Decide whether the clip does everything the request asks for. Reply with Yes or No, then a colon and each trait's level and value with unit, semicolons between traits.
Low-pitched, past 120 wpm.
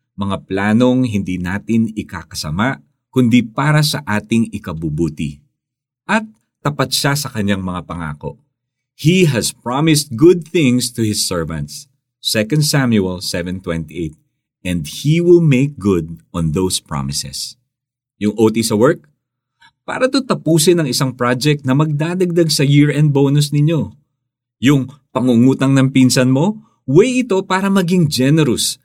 Yes: low, 130 Hz; average, 130 wpm